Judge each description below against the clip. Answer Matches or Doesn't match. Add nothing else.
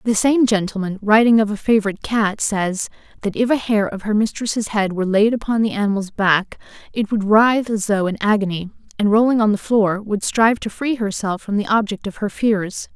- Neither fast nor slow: Doesn't match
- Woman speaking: Matches